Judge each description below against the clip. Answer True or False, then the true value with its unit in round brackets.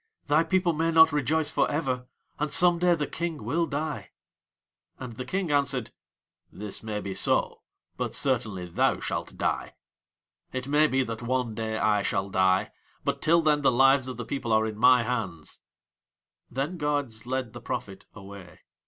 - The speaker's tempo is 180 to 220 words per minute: False (170 wpm)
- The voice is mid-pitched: False (130 Hz)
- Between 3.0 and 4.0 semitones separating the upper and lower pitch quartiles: False (5.4 semitones)